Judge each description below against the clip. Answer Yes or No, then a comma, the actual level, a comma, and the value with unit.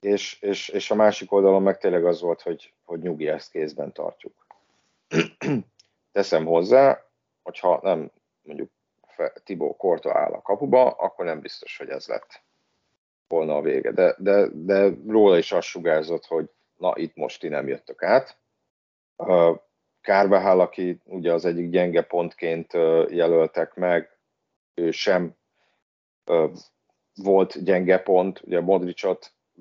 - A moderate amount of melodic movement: Yes, average, 4.0 semitones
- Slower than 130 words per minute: No, average, 135 wpm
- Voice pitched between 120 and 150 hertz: No, very low, 95 Hz